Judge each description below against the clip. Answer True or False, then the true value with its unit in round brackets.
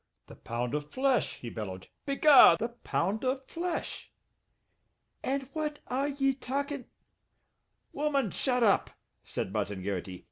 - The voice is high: True (255 Hz)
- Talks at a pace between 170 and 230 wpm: False (140 wpm)